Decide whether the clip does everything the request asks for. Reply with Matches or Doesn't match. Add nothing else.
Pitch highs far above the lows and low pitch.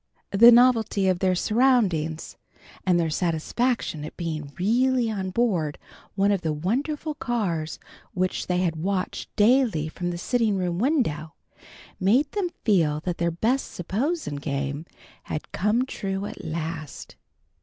Doesn't match